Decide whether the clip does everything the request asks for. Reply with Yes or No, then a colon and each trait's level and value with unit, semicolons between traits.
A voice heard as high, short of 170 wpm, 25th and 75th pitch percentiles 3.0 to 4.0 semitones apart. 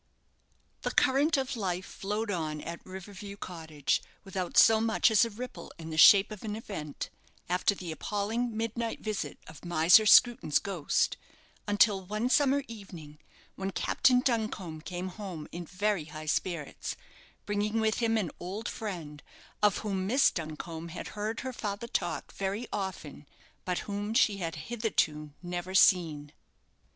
No: high, 195 Hz; average, 150 wpm; average, 4.5 semitones